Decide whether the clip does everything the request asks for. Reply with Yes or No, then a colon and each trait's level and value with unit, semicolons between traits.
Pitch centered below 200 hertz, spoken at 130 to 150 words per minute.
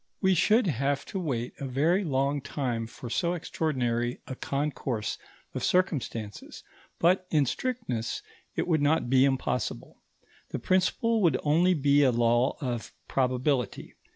Yes: medium, 140 Hz; average, 140 wpm